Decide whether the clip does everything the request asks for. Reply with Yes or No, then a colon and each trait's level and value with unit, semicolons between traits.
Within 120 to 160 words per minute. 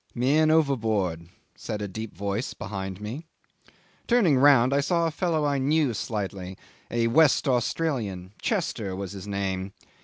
Yes: average, 145 wpm